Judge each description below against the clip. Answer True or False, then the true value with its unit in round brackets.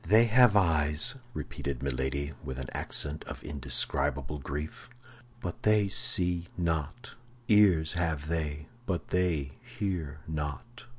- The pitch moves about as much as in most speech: True (4.1 semitones)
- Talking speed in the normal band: False (120 wpm)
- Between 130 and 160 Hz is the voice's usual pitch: False (80 Hz)